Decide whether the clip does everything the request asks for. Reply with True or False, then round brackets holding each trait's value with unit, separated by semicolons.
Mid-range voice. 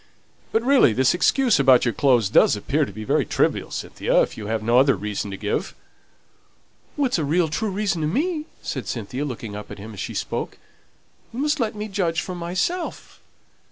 True (150 Hz)